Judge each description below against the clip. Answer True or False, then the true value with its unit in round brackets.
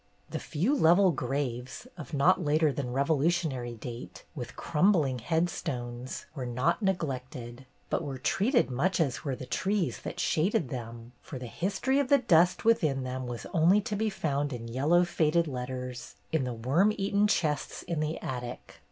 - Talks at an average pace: True (165 wpm)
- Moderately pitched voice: True (145 Hz)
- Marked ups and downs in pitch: True (5.7 semitones)